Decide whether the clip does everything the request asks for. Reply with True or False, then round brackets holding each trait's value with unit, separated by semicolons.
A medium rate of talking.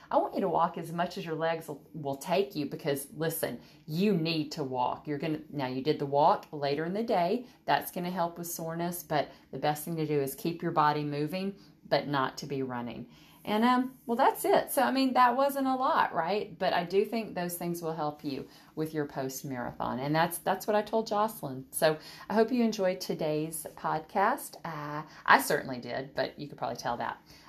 False (225 wpm)